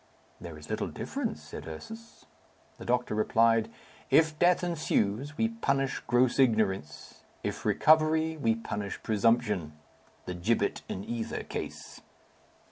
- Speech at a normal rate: No, slow, 125 wpm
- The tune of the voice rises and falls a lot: Yes, wide, 7.5 semitones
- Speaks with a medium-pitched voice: No, low, 115 Hz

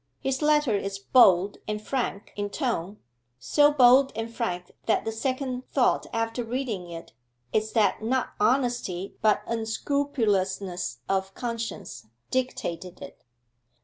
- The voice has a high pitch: Yes, high, 225 Hz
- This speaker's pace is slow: Yes, slow, 125 wpm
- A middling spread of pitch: Yes, average, 4.7 semitones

